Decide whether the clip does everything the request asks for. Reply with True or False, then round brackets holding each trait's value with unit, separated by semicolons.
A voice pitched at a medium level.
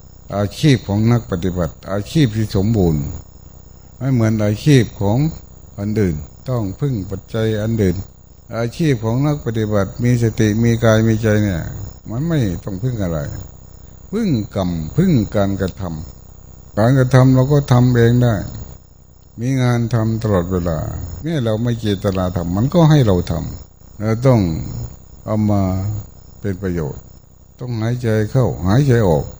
False (110 Hz)